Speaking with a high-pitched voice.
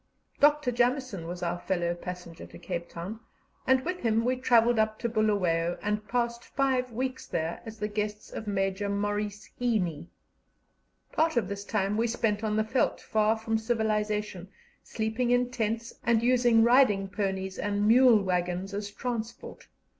Yes: high, 215 Hz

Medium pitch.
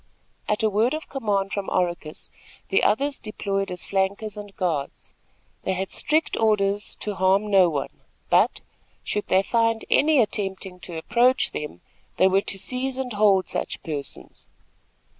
No: high, 200 Hz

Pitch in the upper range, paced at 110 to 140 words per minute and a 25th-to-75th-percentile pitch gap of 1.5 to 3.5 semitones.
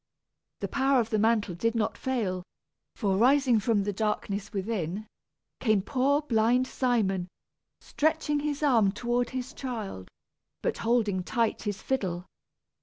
No: high, 225 Hz; slow, 135 wpm; average, 4.2 semitones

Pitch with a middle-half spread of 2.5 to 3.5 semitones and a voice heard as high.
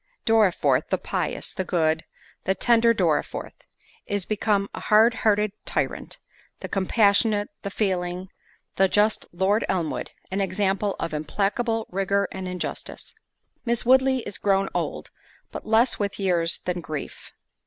Yes: average, 2.8 semitones; high, 200 Hz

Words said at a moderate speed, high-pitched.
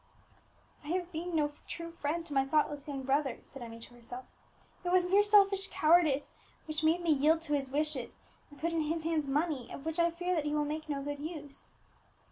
No: fast, 215 wpm; very high, 310 Hz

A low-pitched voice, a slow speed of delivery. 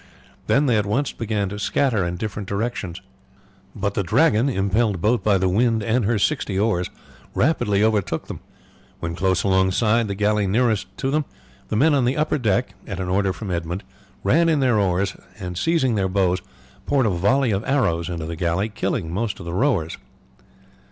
No: low, 105 Hz; average, 185 wpm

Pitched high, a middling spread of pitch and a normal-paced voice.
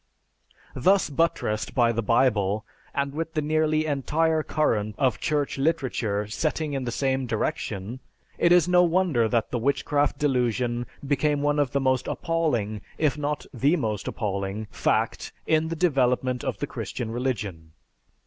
No: low, 135 Hz; average, 5.0 semitones; average, 150 wpm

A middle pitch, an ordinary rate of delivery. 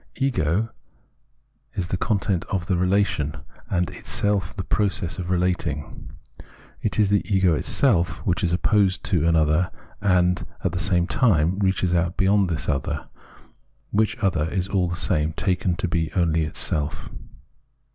No: very low, 90 Hz; average, 145 wpm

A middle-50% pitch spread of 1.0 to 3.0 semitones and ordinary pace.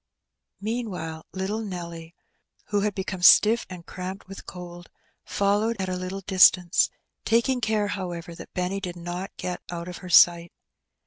Yes: narrow, 2.6 semitones; average, 150 wpm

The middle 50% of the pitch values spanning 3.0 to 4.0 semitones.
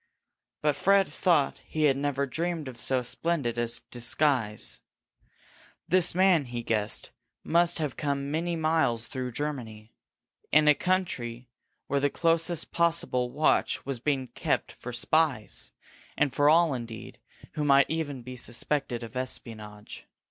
No: average, 4.8 semitones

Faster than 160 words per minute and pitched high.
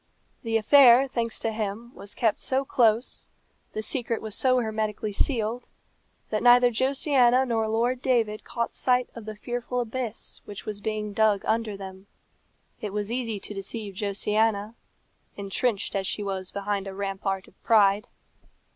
No: average, 155 wpm; high, 220 Hz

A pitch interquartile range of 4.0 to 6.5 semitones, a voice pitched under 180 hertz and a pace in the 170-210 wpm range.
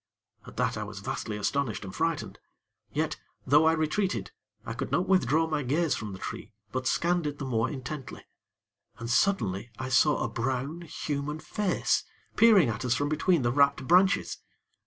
Yes: average, 5.1 semitones; medium, 140 Hz; average, 175 wpm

